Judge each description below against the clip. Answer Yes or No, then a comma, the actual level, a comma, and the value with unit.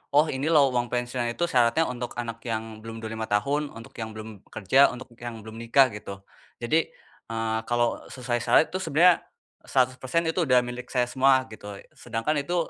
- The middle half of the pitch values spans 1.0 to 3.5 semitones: Yes, average, 3.2 semitones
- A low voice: Yes, low, 120 Hz